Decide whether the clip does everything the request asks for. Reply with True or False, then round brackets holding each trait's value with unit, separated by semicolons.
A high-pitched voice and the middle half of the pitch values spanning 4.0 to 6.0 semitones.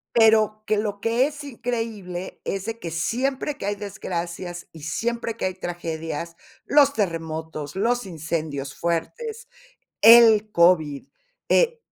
True (200 Hz; 5.6 semitones)